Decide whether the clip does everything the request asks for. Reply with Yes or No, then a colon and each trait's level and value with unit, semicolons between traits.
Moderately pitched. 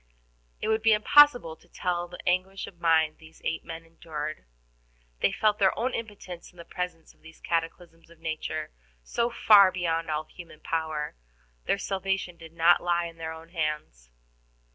Yes: medium, 170 Hz